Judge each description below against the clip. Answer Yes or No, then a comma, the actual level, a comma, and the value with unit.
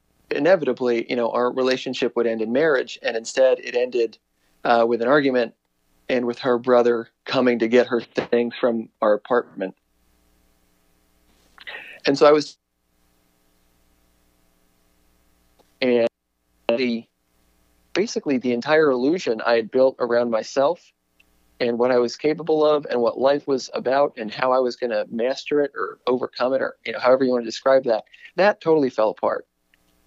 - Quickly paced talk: No, average, 160 wpm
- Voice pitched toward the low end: Yes, low, 115 Hz